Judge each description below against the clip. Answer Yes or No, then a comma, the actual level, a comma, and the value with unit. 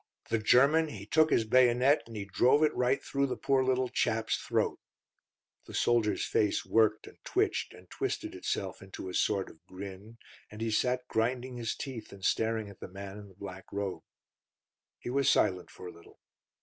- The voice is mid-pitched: No, low, 110 Hz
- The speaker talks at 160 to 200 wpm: Yes, average, 190 wpm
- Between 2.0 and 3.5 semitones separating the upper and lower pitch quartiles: No, average, 4.2 semitones